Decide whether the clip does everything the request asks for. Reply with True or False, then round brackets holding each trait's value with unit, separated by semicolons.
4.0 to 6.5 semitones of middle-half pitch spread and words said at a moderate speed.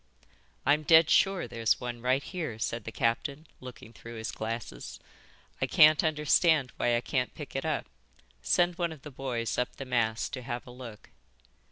True (4.5 semitones; 180 wpm)